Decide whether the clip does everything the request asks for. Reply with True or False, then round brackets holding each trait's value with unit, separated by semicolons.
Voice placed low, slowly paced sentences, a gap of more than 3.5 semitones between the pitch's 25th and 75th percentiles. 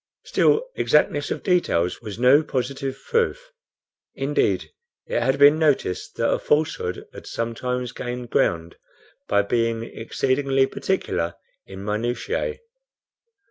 True (125 Hz; 115 wpm; 4.4 semitones)